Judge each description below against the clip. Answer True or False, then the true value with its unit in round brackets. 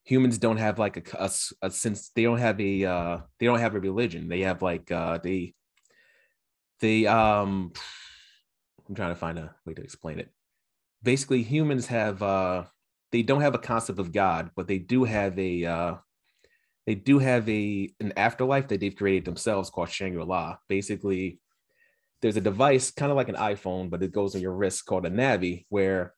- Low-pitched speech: True (100 Hz)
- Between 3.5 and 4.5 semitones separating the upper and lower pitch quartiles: True (4.1 semitones)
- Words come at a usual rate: True (195 wpm)